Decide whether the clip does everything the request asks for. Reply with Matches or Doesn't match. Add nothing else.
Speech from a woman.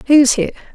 Matches